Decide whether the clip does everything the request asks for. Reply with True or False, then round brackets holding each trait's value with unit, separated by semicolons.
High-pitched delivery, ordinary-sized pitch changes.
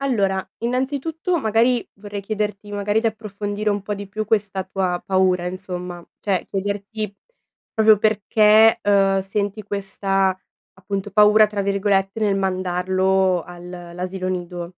False (200 Hz; 2.1 semitones)